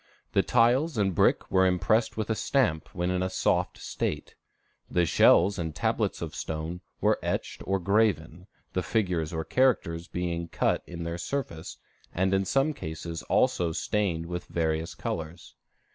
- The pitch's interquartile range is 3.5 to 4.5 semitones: Yes, average, 3.9 semitones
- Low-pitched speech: Yes, very low, 90 Hz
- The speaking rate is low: No, average, 160 wpm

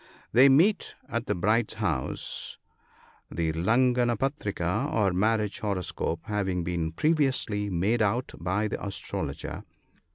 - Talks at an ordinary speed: No, slow, 125 wpm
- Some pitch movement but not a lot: Yes, average, 5.0 semitones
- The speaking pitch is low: Yes, low, 105 Hz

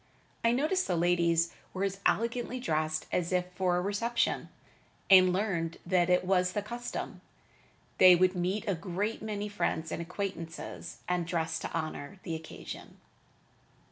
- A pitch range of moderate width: Yes, average, 3.3 semitones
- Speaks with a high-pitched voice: No, medium, 180 Hz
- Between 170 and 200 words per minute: No, average, 150 wpm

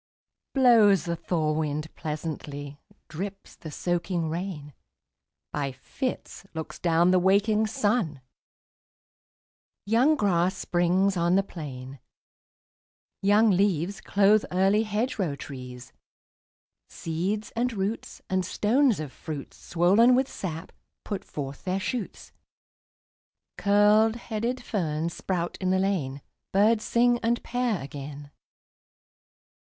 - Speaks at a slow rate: Yes, slow, 110 wpm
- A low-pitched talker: No, medium, 185 Hz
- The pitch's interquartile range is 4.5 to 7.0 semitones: Yes, average, 5.2 semitones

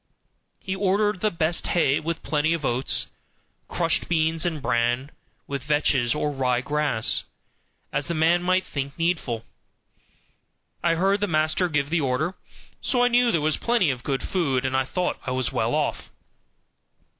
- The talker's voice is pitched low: No, medium, 155 Hz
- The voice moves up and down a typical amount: Yes, average, 4.6 semitones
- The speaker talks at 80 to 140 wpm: No, average, 165 wpm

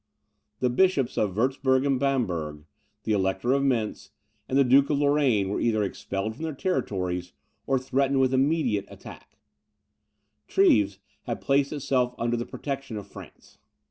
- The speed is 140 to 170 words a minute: Yes, average, 150 wpm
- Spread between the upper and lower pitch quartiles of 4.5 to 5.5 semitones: Yes, average, 4.8 semitones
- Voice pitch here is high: No, low, 130 Hz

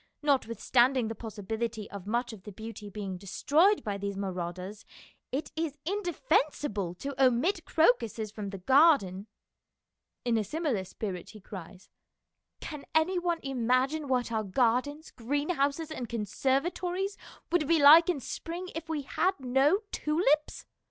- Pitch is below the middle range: No, very high, 255 Hz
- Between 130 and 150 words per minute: Yes, average, 145 wpm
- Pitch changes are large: Yes, wide, 6.8 semitones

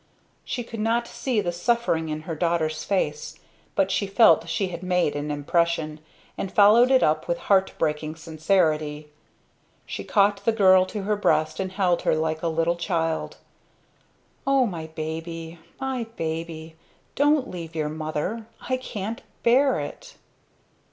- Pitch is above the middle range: No, medium, 170 Hz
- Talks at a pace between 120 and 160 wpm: Yes, average, 150 wpm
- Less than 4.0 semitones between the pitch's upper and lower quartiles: No, average, 4.8 semitones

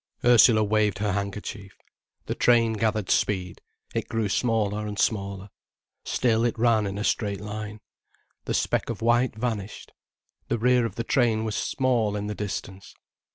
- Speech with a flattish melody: Yes, narrow, 2.2 semitones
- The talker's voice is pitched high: No, low, 110 Hz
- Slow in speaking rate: No, average, 155 wpm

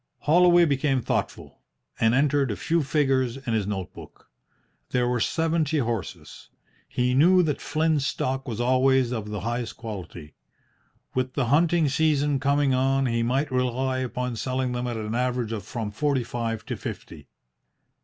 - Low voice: Yes, low, 130 Hz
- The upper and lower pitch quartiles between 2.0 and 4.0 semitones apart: Yes, average, 3.5 semitones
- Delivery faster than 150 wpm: Yes, average, 160 wpm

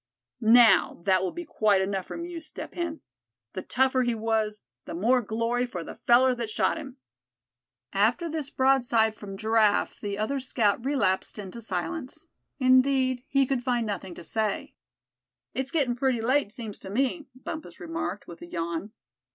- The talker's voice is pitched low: No, high, 235 Hz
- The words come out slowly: No, average, 165 wpm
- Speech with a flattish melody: No, average, 4.3 semitones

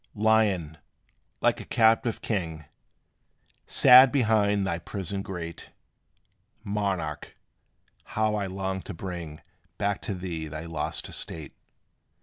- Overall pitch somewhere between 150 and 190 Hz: No, very low, 95 Hz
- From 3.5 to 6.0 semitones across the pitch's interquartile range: Yes, average, 4.2 semitones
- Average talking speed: No, slow, 110 wpm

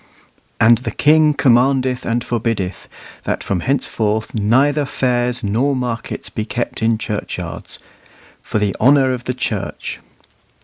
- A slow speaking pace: Yes, slow, 130 wpm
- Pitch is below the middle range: Yes, low, 120 Hz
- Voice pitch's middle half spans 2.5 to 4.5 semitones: Yes, average, 3.0 semitones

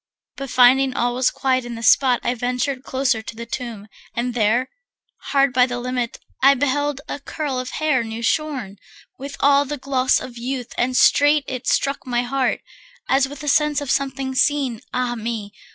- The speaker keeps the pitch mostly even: Yes, narrow, 2.3 semitones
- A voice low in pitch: No, very high, 255 Hz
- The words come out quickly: No, average, 185 wpm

